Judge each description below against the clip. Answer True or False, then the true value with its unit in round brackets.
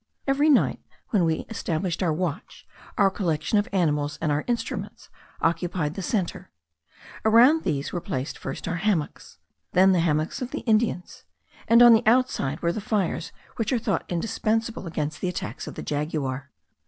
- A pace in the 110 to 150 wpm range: False (165 wpm)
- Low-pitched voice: False (180 Hz)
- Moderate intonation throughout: False (6.1 semitones)